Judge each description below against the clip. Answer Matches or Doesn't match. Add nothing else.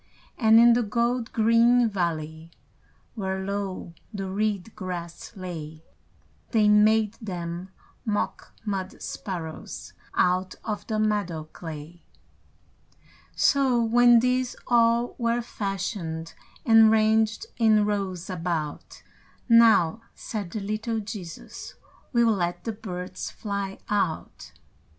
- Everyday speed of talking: Doesn't match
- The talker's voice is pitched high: Matches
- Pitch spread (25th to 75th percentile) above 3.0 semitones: Matches